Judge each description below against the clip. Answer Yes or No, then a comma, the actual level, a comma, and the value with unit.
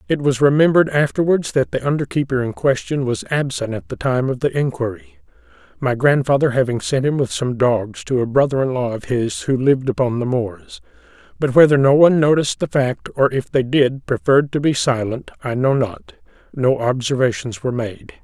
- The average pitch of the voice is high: No, low, 130 Hz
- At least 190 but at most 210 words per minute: Yes, average, 195 wpm